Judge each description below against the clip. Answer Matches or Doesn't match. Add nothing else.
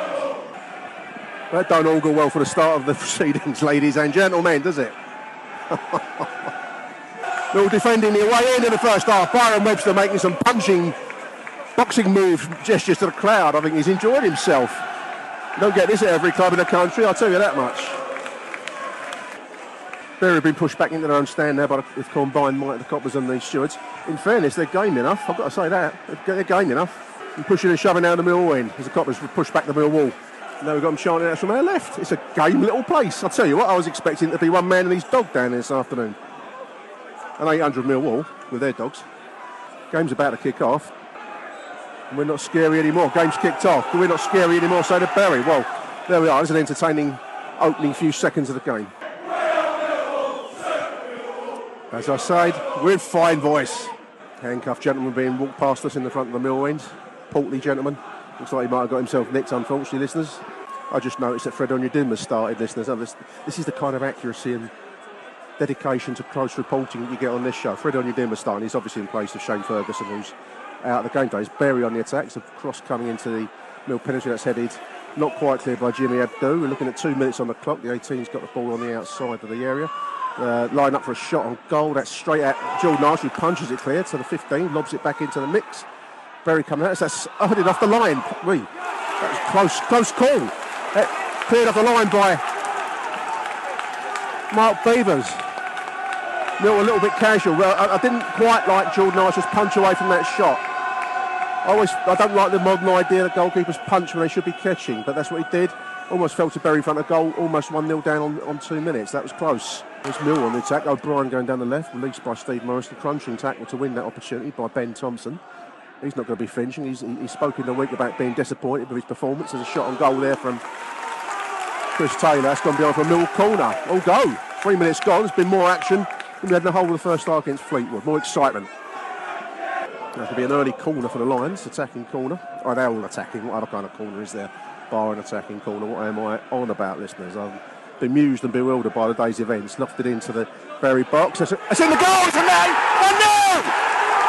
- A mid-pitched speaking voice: Matches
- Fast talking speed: Matches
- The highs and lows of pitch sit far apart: Matches